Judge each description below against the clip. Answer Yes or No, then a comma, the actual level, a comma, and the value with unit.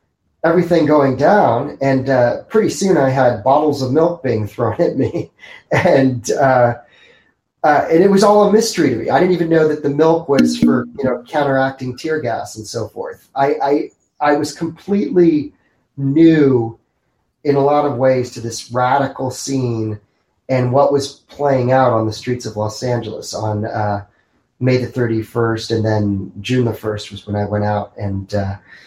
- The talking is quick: No, average, 185 wpm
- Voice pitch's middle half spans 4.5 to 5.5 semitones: Yes, average, 4.9 semitones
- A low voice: Yes, low, 125 Hz